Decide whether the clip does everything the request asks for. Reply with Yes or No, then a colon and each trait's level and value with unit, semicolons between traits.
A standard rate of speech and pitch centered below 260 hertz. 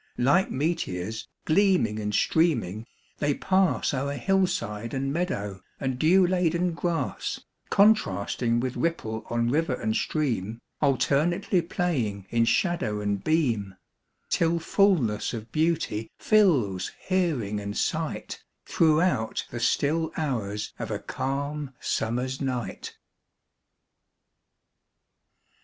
No: slow, 105 wpm; low, 135 Hz